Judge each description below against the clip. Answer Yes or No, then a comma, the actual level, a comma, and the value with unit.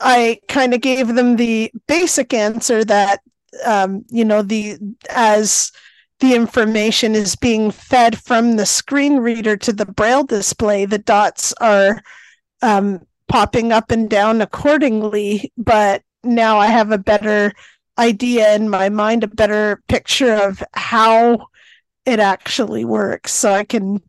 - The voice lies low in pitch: No, high, 220 Hz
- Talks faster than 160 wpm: No, average, 140 wpm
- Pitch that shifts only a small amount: Yes, narrow, 2.3 semitones